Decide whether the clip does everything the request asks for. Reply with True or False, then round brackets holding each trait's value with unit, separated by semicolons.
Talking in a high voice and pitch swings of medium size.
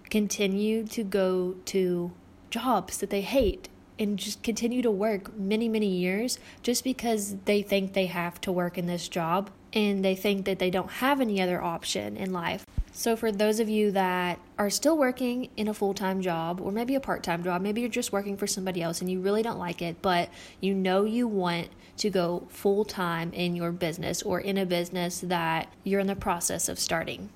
True (195 Hz; 3.0 semitones)